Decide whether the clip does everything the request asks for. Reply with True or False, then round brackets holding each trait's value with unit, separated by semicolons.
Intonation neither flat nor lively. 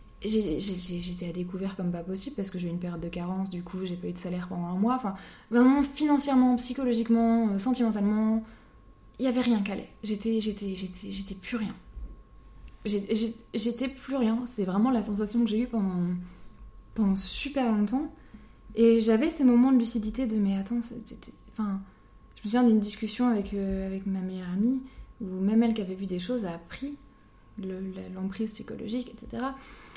True (3.8 semitones)